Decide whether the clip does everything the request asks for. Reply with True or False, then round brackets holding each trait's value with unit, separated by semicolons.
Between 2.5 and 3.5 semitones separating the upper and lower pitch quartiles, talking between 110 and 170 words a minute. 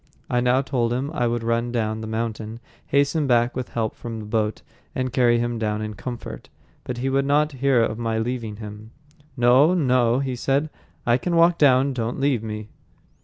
False (3.1 semitones; 195 wpm)